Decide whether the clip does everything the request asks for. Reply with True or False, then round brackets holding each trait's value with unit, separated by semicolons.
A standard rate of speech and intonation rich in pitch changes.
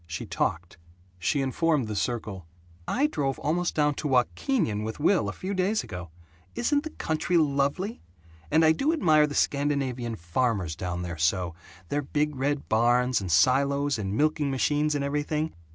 True (165 wpm; 5.9 semitones)